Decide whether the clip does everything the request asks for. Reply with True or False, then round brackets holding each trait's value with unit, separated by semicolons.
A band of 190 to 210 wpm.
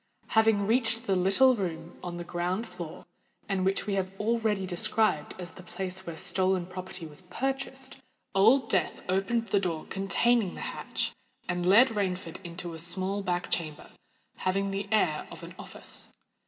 False (165 wpm)